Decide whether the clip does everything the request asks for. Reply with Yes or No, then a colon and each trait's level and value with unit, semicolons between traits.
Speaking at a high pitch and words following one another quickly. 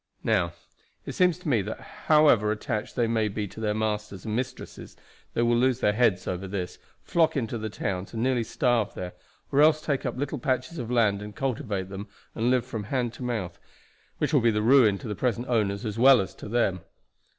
No: low, 115 Hz; fast, 210 wpm